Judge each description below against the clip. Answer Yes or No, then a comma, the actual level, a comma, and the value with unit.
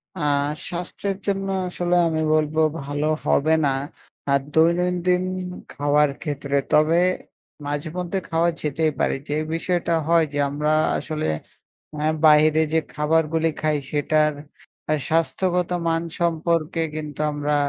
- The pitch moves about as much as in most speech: No, narrow, 2.3 semitones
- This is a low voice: No, medium, 160 Hz